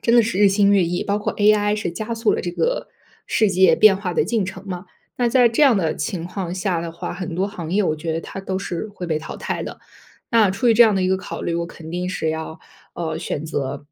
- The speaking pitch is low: No, high, 190 Hz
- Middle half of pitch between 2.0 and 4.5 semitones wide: Yes, average, 3.7 semitones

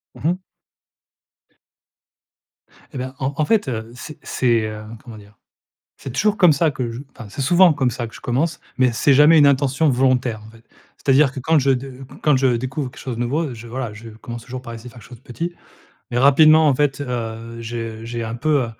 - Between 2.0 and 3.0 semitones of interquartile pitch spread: No, average, 3.6 semitones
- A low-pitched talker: Yes, low, 130 Hz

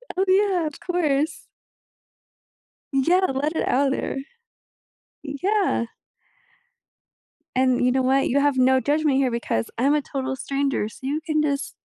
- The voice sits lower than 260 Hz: No, very high, 280 Hz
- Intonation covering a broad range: No, average, 2.9 semitones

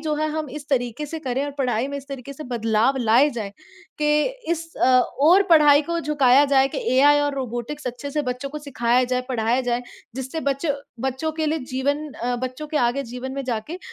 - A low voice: No, very high, 275 Hz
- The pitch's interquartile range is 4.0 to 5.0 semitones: No, average, 3.2 semitones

